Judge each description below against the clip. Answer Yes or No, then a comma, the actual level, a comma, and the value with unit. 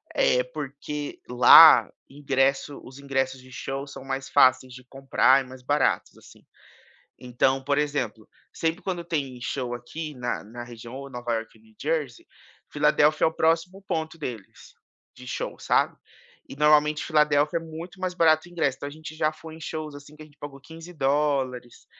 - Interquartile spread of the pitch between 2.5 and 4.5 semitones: Yes, average, 3.3 semitones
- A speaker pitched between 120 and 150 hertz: Yes, medium, 140 Hz